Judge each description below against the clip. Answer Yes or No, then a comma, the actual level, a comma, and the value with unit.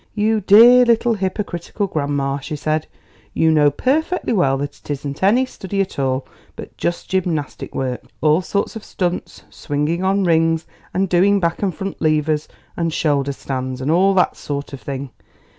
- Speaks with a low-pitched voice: No, medium, 165 Hz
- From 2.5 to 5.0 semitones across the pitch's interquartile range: No, wide, 5.4 semitones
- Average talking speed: Yes, average, 170 wpm